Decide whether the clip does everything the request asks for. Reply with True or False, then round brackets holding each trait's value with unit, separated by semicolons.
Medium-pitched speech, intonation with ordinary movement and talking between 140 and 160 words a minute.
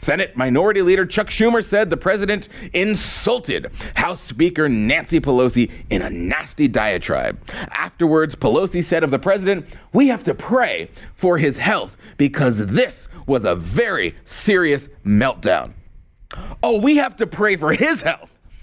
False (180 Hz; 7.0 semitones; 145 wpm)